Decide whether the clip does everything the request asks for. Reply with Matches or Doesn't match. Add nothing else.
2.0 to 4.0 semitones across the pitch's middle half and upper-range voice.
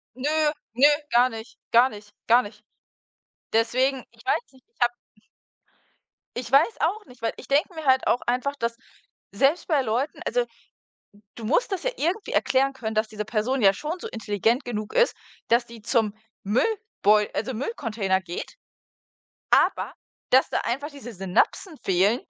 Doesn't match